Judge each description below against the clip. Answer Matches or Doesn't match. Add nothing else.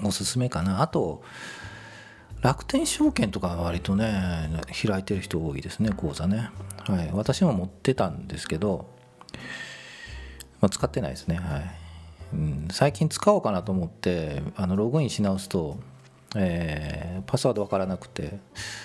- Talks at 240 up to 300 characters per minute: Matches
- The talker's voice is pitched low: Matches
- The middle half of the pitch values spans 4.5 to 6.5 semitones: Matches